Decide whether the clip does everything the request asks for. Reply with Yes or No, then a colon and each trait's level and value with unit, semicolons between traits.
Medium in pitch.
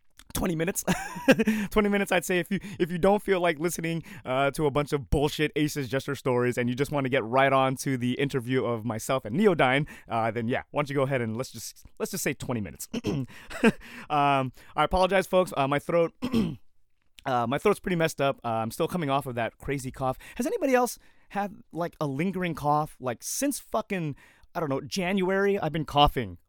Yes: medium, 145 Hz